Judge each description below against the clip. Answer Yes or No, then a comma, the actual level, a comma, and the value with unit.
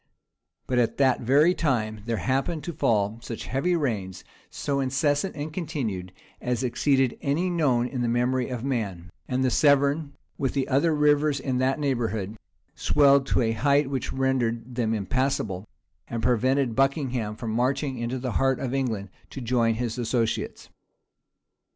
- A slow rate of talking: No, average, 155 wpm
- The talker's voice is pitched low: Yes, low, 130 Hz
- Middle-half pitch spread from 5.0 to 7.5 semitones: No, average, 3.3 semitones